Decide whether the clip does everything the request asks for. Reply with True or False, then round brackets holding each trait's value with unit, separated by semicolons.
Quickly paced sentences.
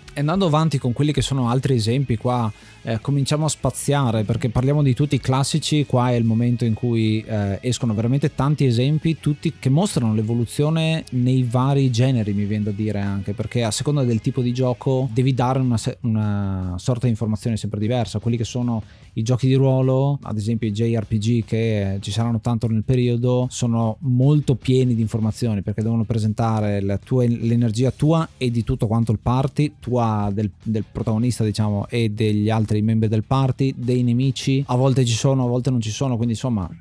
True (190 wpm)